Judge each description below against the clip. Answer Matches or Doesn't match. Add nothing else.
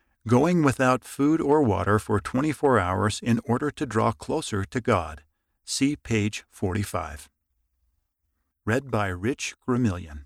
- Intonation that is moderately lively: Doesn't match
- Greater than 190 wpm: Doesn't match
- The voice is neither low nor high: Doesn't match